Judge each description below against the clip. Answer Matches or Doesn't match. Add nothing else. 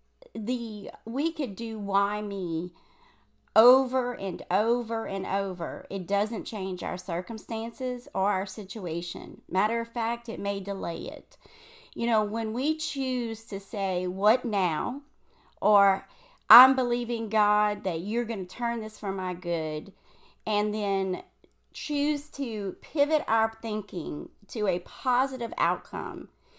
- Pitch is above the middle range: Matches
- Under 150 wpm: Matches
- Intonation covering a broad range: Doesn't match